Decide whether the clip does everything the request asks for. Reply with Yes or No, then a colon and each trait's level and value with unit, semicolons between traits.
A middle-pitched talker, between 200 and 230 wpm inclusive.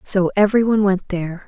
No: high, 195 Hz; fast, 205 wpm